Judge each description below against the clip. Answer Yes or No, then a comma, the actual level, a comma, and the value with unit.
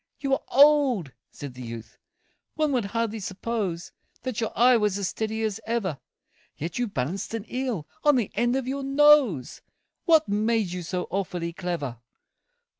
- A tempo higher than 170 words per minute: No, average, 165 wpm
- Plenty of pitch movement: Yes, wide, 6.2 semitones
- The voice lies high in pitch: Yes, high, 220 Hz